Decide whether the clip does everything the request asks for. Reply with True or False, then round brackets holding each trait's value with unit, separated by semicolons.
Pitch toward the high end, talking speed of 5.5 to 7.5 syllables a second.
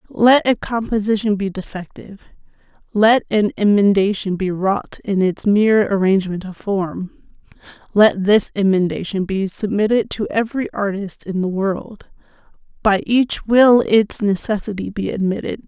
False (205 Hz; 4.6 syllables/s)